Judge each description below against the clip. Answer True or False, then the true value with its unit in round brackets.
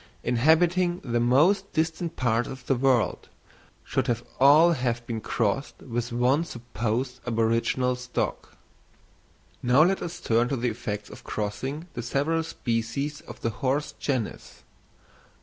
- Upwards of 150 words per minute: False (135 wpm)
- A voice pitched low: True (125 Hz)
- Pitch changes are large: False (4.0 semitones)